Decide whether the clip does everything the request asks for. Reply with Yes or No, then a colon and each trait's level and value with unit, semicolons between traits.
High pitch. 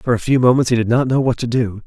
No: low, 120 Hz